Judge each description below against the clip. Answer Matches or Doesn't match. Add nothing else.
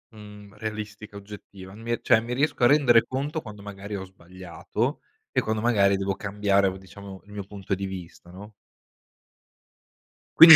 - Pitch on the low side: Matches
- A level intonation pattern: Matches